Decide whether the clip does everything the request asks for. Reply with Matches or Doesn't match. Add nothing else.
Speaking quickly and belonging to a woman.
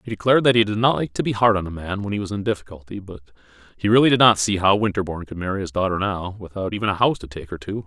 Doesn't match